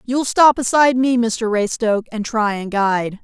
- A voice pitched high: Yes, high, 230 Hz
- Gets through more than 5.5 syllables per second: No, 5.1 syllables/s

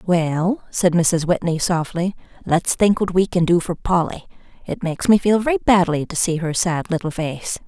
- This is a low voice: No, medium, 175 Hz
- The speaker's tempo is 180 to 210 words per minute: Yes, average, 195 wpm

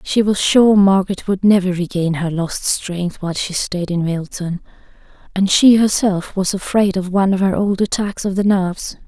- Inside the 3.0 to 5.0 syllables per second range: Yes, 4.9 syllables/s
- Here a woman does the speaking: Yes, female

